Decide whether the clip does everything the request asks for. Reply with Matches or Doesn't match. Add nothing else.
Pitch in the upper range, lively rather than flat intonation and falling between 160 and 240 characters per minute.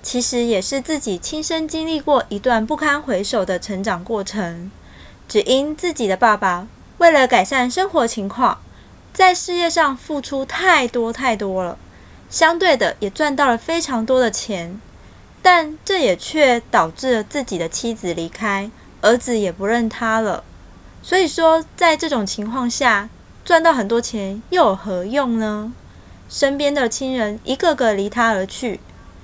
Matches